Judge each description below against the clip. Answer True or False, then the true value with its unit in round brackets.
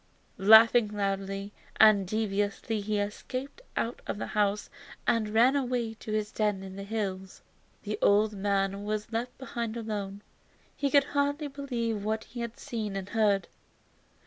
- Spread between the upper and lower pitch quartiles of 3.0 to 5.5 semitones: False (2.6 semitones)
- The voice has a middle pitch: False (215 Hz)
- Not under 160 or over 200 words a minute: False (150 wpm)